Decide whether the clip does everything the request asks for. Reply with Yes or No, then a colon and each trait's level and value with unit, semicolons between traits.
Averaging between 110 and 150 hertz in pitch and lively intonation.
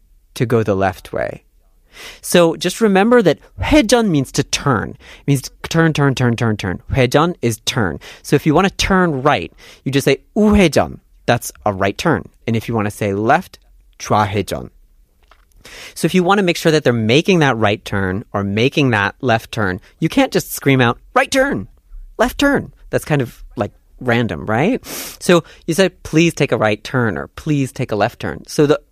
Yes: medium, 140 Hz; wide, 8.4 semitones